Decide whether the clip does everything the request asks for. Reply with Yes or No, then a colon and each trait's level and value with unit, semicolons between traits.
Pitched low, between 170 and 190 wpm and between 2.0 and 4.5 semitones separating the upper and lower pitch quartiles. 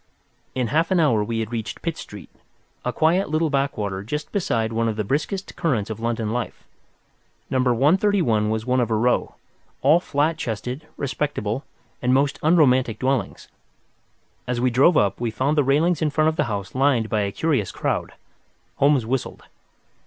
No: low, 130 Hz; average, 175 wpm; average, 5.3 semitones